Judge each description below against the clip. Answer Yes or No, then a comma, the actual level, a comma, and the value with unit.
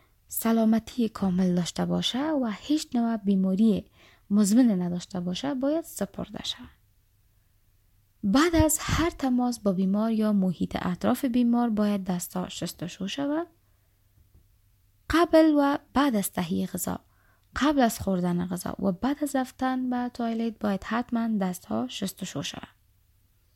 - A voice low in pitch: No, high, 200 Hz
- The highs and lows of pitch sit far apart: Yes, wide, 7.6 semitones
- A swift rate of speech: No, average, 130 wpm